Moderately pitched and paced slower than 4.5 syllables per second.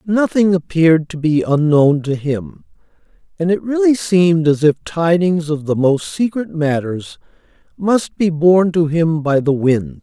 Yes: medium, 165 Hz; 4.3 syllables/s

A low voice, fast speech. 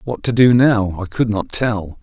Yes: low, 110 Hz; fast, 235 wpm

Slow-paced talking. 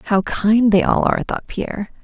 No: fast, 205 wpm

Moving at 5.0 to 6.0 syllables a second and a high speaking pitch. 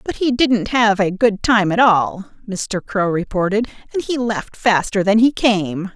No: 4.2 syllables/s; high, 210 Hz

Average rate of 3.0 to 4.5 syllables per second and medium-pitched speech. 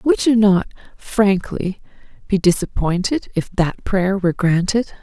No: 4.1 syllables/s; high, 195 Hz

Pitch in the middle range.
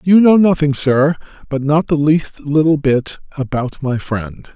Yes: medium, 145 Hz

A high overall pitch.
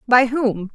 Yes: high, 240 Hz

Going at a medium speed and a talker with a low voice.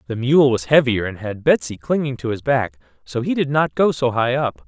No: fast, 245 wpm; low, 125 Hz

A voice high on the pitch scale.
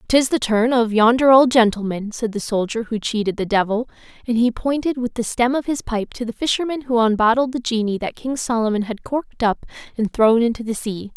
Yes: high, 235 Hz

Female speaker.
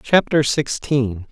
No: male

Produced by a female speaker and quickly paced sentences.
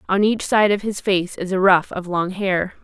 Yes: female; fast, 255 wpm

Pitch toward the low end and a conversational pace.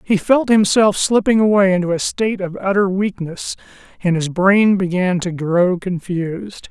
No: high, 190 Hz; average, 160 wpm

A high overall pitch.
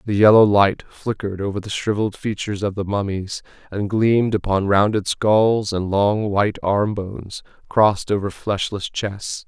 No: low, 100 Hz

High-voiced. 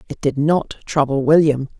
No: medium, 145 Hz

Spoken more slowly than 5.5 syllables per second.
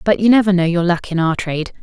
No: 6.7 syllables/s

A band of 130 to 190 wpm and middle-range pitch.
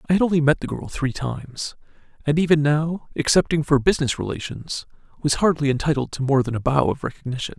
No: average, 200 wpm; medium, 145 Hz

